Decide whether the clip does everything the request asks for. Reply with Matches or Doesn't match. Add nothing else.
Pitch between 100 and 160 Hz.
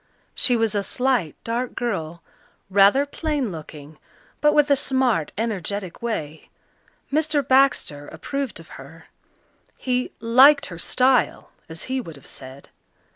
Doesn't match